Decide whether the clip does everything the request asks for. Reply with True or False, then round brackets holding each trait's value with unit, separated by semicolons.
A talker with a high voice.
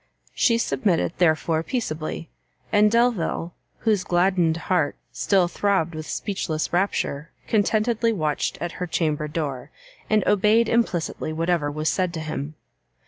False (175 Hz)